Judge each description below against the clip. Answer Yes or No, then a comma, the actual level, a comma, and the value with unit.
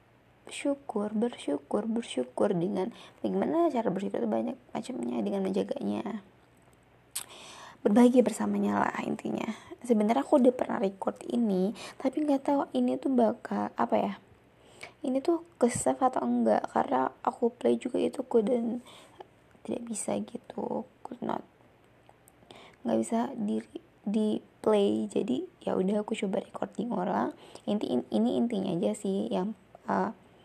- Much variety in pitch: No, average, 4.1 semitones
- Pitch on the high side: Yes, high, 225 Hz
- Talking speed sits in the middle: Yes, average, 130 wpm